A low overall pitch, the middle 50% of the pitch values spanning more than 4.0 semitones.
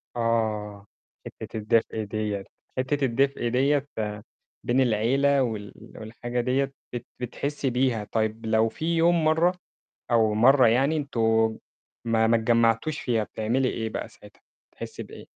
No: low, 120 Hz; average, 3.4 semitones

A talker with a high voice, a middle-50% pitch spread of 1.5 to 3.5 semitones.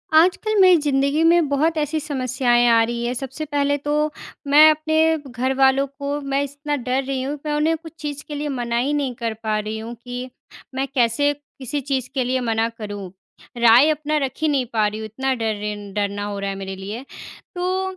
No: very high, 265 Hz; average, 4.2 semitones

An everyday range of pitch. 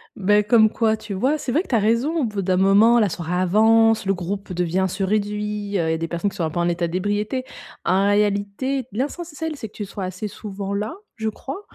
Yes: average, 3.0 semitones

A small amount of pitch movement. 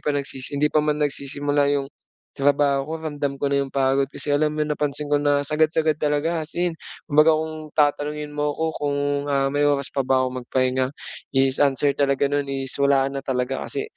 Yes: narrow, 1.6 semitones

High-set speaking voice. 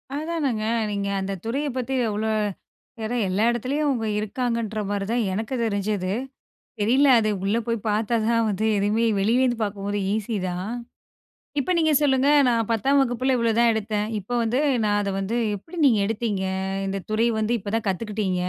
Yes: high, 220 Hz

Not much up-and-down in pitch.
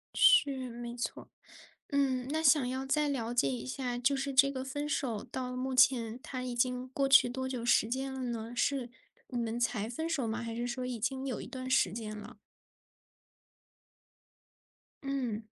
Yes: narrow, 2.2 semitones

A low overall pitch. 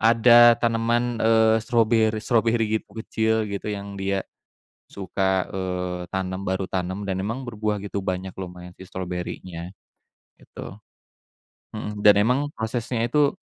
Yes: low, 105 Hz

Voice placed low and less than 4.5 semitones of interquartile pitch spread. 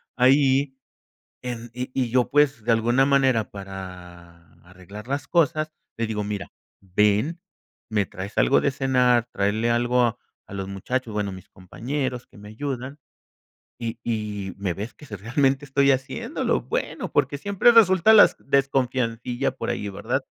No: low, 120 Hz; average, 4.8 semitones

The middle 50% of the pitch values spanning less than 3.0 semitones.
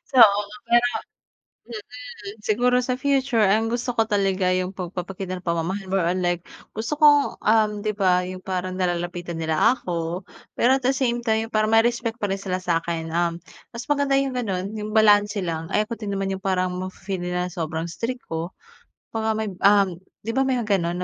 No: average, 4.0 semitones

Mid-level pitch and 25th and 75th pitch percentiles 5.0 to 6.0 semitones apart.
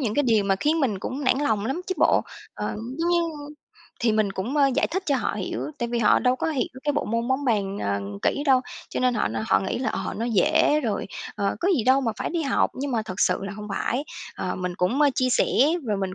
No: high, 240 Hz; average, 5.3 semitones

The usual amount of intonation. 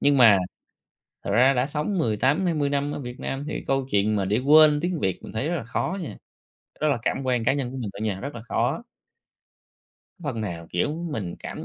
Yes: average, 4.8 semitones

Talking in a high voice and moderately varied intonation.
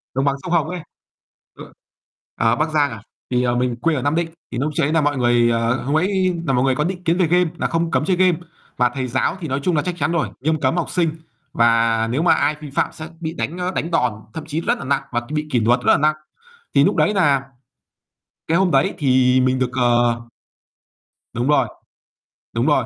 No: medium, 145 Hz; average, 4.9 semitones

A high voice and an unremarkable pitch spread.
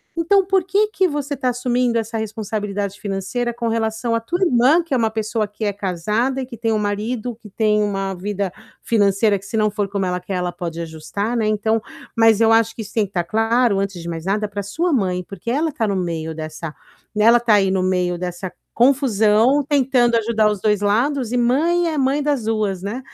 Yes: high, 220 Hz; average, 3.7 semitones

